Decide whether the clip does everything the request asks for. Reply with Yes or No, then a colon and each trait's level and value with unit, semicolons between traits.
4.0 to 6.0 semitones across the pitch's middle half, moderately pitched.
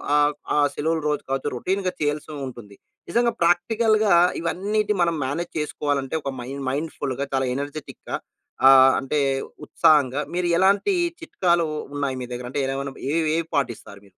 Yes: average, 4.4 semitones; medium, 150 Hz